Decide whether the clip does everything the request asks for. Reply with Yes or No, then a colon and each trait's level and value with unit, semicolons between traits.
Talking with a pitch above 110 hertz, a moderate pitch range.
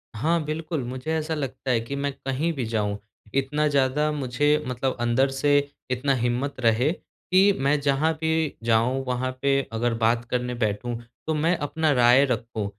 Yes: low, 135 Hz; average, 3.5 semitones